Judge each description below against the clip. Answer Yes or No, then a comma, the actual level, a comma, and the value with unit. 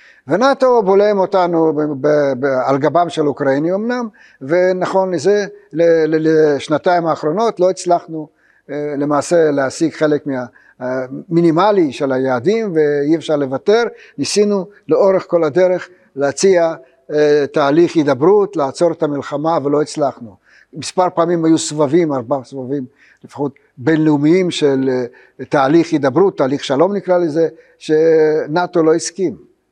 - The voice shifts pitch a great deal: No, average, 3.9 semitones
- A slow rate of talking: No, average, 115 wpm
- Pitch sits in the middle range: Yes, medium, 160 Hz